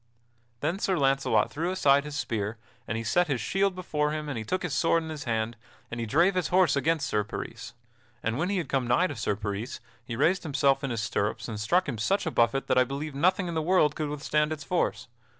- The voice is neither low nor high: Yes, medium, 145 Hz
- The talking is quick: Yes, fast, 240 wpm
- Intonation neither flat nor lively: No, wide, 6.1 semitones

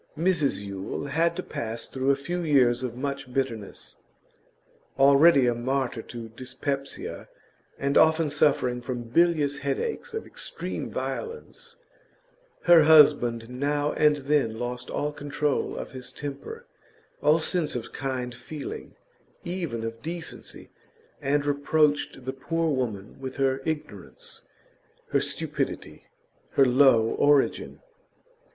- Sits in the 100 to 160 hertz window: Yes, medium, 140 Hz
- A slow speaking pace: Yes, slow, 120 wpm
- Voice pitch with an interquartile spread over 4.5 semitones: No, average, 3.4 semitones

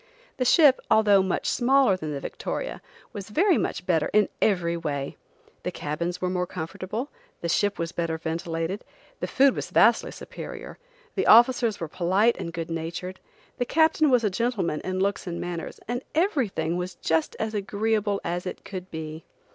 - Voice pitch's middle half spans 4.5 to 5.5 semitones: Yes, average, 5.1 semitones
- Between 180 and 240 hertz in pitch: Yes, medium, 185 Hz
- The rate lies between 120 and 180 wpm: Yes, average, 170 wpm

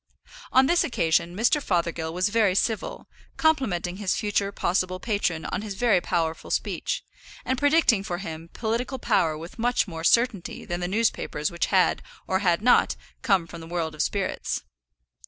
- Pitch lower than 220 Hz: Yes, high, 190 Hz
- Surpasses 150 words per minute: Yes, average, 165 wpm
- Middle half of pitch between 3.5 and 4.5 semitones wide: No, average, 5.0 semitones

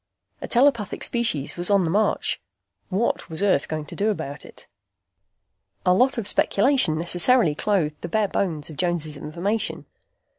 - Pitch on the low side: No, medium, 185 Hz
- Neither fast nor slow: Yes, average, 155 wpm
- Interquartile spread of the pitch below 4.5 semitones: No, wide, 5.5 semitones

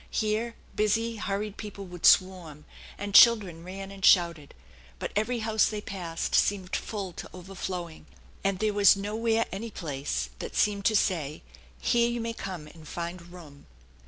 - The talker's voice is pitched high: Yes, high, 195 Hz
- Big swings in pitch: No, average, 3.8 semitones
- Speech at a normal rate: Yes, average, 160 wpm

